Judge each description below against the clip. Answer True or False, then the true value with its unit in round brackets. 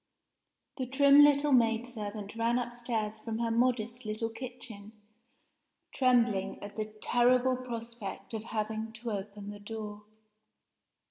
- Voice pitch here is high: True (230 Hz)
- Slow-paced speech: True (125 wpm)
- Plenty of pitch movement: False (2.4 semitones)